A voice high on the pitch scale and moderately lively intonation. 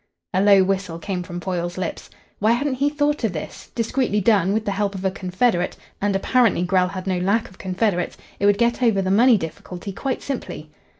Yes: high, 195 Hz; average, 3.8 semitones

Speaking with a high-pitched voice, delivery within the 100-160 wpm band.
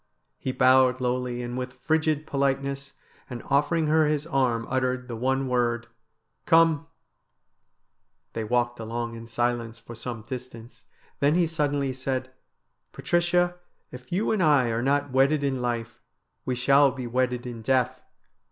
No: low, 130 Hz; average, 155 wpm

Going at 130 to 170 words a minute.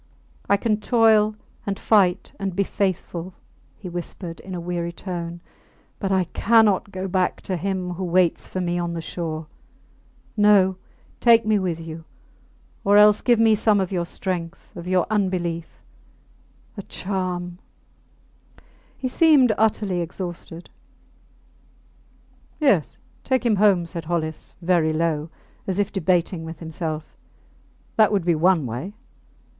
Yes: average, 140 wpm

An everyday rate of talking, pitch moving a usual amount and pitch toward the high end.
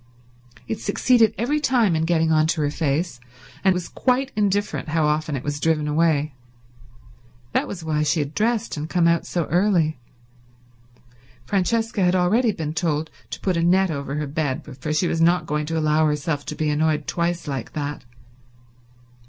No: average, 175 wpm; average, 3.5 semitones; medium, 160 Hz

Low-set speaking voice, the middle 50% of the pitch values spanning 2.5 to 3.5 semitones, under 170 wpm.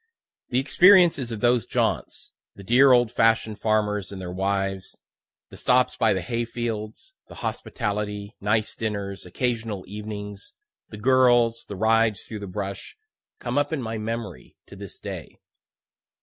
Yes: low, 110 Hz; average, 3.0 semitones; average, 150 wpm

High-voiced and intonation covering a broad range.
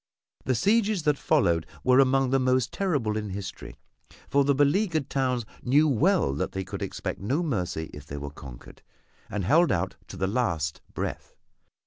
No: low, 130 Hz; wide, 7.5 semitones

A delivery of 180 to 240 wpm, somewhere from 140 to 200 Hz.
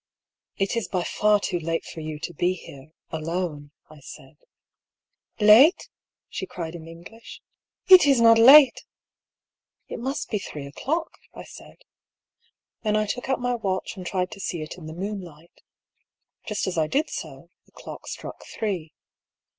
Yes: average, 185 wpm; high, 190 Hz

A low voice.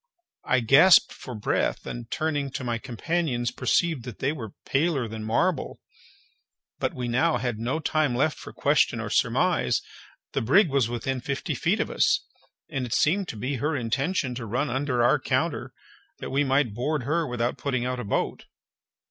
Yes: low, 130 Hz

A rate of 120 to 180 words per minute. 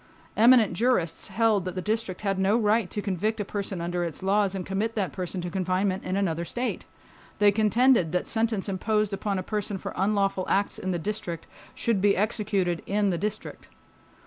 No: average, 190 wpm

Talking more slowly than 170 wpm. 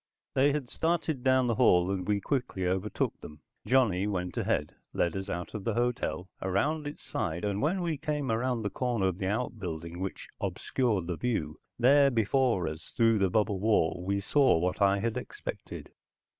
No: average, 185 wpm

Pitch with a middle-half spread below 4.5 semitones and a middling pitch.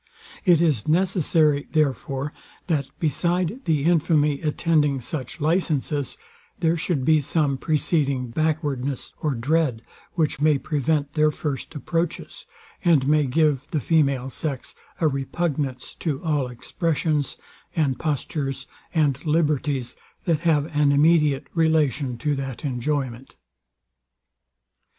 Yes: average, 2.8 semitones; medium, 150 Hz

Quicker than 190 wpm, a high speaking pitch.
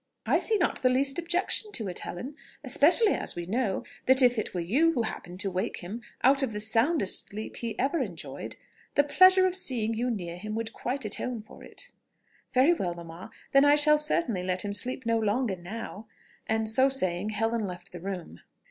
Yes: average, 200 wpm; high, 230 Hz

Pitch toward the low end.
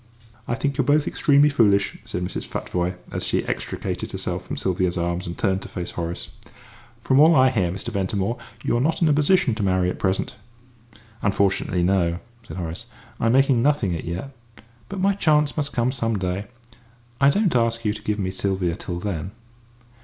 Yes: low, 105 Hz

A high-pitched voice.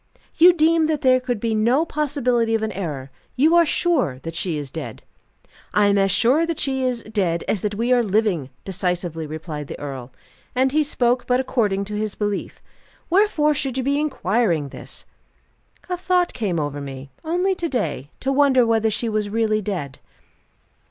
Yes: high, 225 Hz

